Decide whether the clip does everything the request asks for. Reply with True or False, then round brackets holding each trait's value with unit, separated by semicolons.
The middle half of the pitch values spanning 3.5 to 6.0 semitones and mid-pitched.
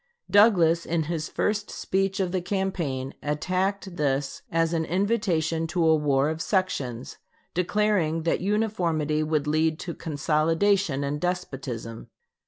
True (3.9 semitones; 165 Hz)